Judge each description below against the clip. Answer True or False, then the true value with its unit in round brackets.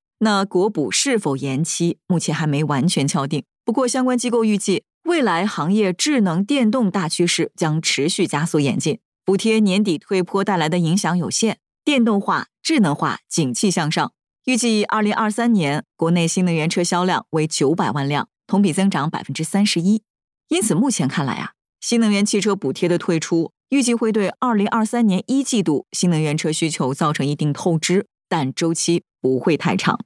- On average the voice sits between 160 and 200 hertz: True (185 Hz)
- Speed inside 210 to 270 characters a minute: False (285 characters per minute)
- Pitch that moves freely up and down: False (5.0 semitones)